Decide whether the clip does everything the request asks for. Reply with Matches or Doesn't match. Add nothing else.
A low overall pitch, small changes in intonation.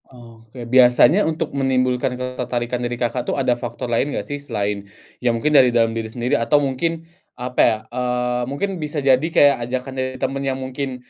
Matches